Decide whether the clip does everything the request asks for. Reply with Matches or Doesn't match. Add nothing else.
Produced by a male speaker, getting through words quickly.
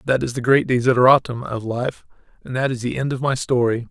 Matches